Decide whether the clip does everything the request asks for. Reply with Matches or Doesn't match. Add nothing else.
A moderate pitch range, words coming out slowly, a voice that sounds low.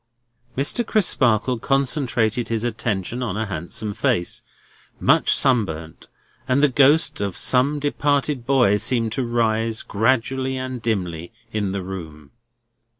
Matches